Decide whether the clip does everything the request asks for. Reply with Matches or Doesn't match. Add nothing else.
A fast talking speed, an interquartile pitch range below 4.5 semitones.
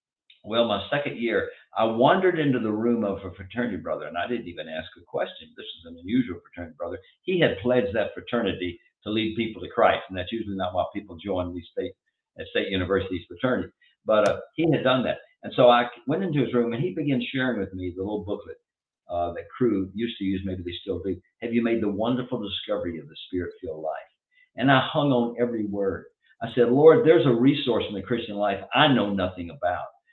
Doesn't match